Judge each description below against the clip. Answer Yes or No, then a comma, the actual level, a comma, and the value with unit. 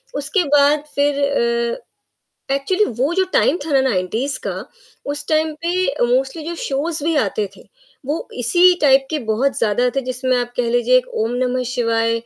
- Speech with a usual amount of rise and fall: Yes, average, 3.7 semitones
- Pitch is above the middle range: Yes, very high, 270 Hz